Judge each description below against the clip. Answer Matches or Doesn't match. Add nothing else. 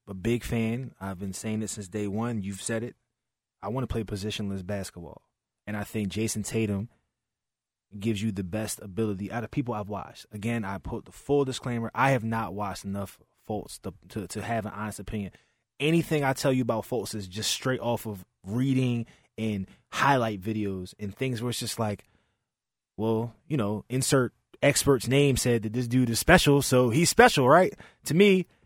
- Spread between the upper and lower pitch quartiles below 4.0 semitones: Matches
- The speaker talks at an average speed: Matches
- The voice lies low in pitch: Matches